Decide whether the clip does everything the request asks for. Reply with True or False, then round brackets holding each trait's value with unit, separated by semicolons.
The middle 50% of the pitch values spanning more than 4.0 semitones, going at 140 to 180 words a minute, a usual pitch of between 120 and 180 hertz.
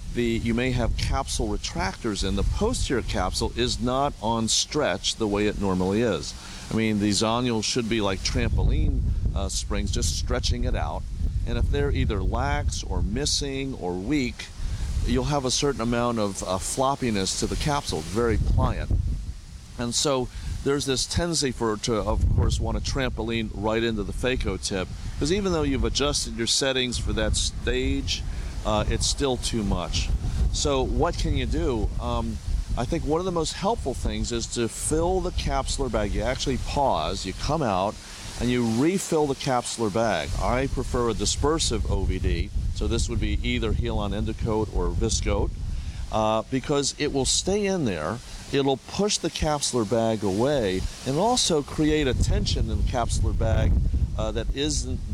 False (5.0 semitones; 175 wpm; 110 Hz)